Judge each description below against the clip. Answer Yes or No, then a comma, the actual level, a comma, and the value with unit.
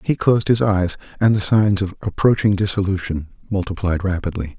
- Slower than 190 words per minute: Yes, average, 155 wpm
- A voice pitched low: Yes, very low, 95 Hz